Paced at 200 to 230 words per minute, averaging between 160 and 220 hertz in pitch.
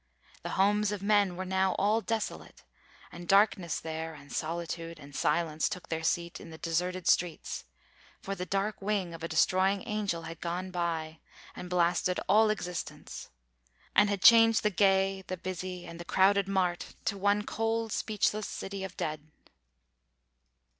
No: average, 160 wpm; medium, 185 Hz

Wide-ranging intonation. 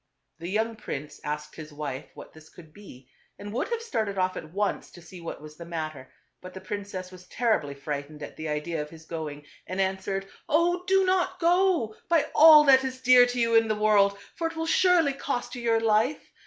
Yes: wide, 8.4 semitones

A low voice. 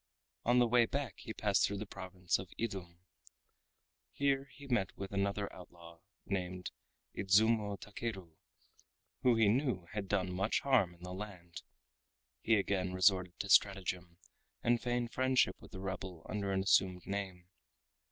Yes: low, 100 Hz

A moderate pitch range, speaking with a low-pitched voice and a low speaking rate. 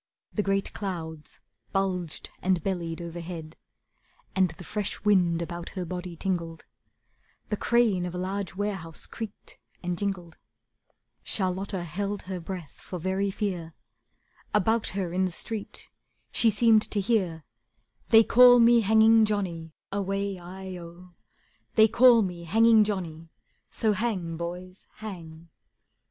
No: average, 3.3 semitones; high, 190 Hz; slow, 130 wpm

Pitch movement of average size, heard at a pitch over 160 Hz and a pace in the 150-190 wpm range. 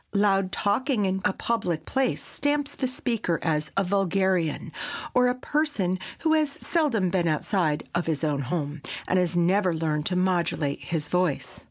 No: wide, 5.8 semitones; medium, 185 Hz; average, 165 wpm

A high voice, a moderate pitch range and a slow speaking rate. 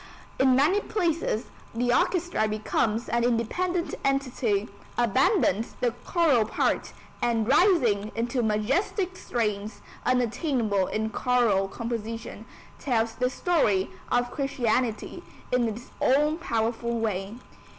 Yes: high, 240 Hz; average, 3.8 semitones; slow, 110 wpm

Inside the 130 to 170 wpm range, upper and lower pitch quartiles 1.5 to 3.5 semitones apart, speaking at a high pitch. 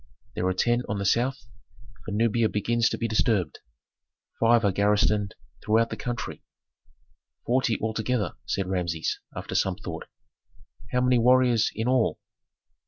No: average, 140 wpm; average, 2.9 semitones; low, 110 Hz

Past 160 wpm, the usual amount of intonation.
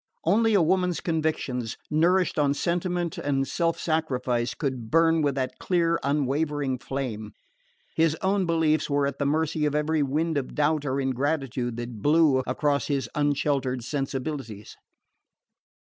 No: average, 140 wpm; average, 3.4 semitones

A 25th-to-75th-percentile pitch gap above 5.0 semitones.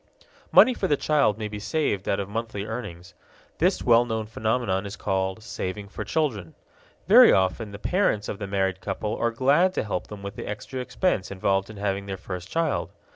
No: average, 3.6 semitones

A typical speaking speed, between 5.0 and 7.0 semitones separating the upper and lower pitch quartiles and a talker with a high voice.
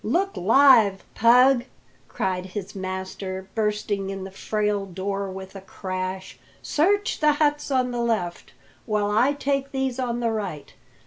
Yes: average, 145 wpm; wide, 5.4 semitones; high, 210 Hz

